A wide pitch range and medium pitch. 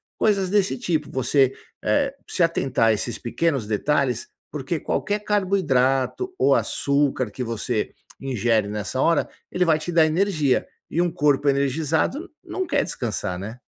Yes: wide, 6.0 semitones; medium, 145 Hz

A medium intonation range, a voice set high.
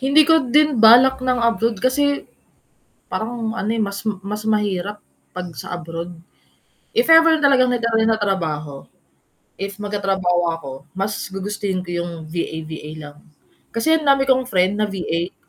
No: wide, 5.8 semitones; high, 210 Hz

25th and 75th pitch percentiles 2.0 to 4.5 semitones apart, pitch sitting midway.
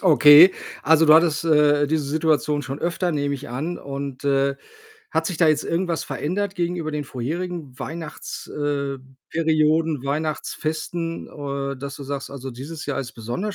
Yes: average, 2.8 semitones; medium, 150 Hz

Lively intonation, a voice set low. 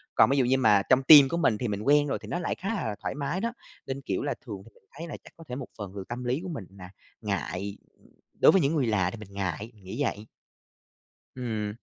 Yes: wide, 5.8 semitones; low, 125 Hz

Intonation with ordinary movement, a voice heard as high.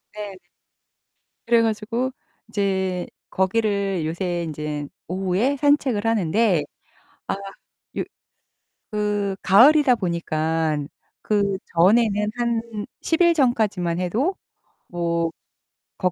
Yes: average, 4.6 semitones; high, 200 Hz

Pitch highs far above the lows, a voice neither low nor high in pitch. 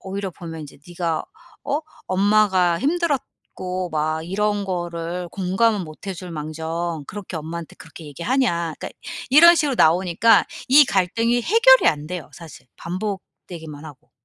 No: average, 4.4 semitones; medium, 180 Hz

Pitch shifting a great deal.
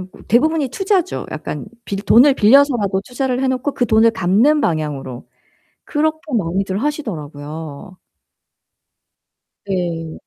Yes: wide, 8.8 semitones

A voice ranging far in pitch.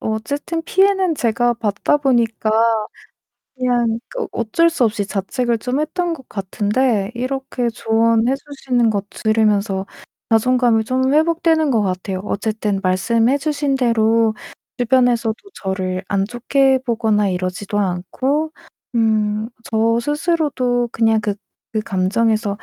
No: average, 3.9 semitones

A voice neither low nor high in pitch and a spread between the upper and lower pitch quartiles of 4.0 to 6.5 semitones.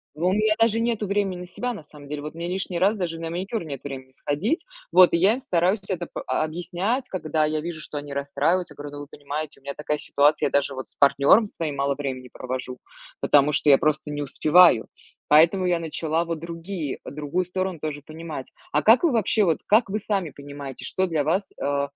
Yes: medium, 165 Hz; average, 4.5 semitones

